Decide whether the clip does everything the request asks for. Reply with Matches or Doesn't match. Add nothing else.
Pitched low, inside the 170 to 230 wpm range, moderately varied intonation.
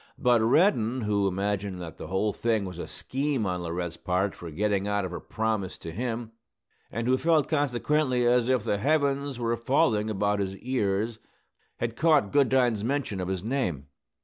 Matches